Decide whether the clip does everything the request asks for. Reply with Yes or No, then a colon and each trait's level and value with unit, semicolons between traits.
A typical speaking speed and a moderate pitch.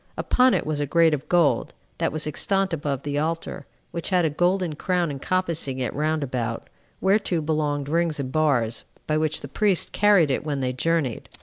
Yes: average, 190 wpm; medium, 155 Hz